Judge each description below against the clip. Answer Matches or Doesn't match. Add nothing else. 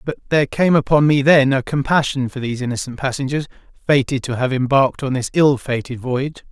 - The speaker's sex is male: Matches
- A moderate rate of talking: Matches